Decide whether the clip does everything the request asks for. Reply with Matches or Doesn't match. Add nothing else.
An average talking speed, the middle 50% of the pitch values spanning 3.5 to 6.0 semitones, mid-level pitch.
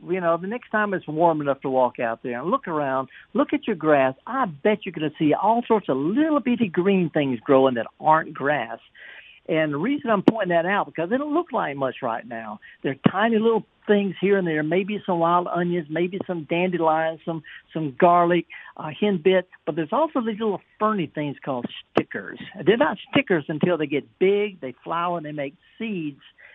Doesn't match